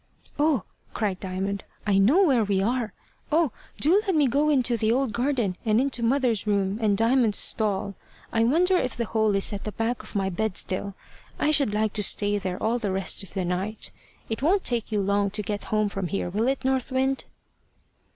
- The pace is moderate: No, fast, 210 wpm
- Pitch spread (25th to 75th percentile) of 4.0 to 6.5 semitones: Yes, average, 4.5 semitones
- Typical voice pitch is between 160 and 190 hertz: No, high, 220 Hz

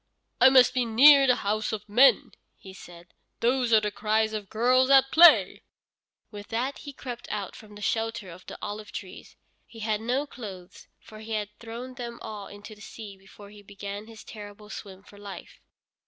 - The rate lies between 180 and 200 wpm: Yes, average, 190 wpm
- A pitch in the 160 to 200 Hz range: No, high, 215 Hz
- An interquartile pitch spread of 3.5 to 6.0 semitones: No, average, 2.9 semitones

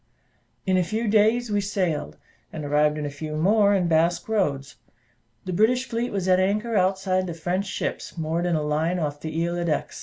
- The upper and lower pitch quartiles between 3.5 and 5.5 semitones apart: Yes, average, 4.5 semitones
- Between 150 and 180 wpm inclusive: No, average, 200 wpm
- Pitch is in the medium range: Yes, medium, 180 Hz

